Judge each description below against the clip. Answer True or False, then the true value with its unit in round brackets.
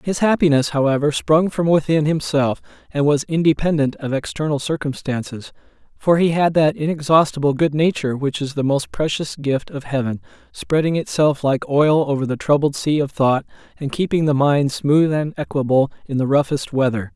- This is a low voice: False (145 Hz)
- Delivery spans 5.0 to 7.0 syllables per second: True (5.2 syllables/s)